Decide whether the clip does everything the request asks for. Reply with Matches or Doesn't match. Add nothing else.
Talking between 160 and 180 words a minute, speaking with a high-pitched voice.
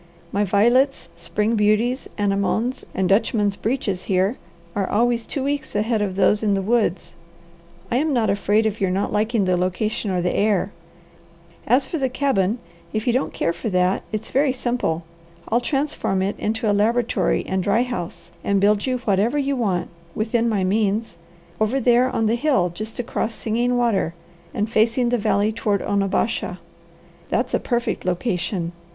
Matches